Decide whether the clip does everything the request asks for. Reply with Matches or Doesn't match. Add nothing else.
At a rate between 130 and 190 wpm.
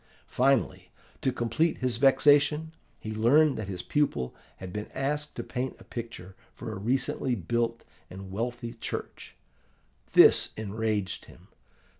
Matches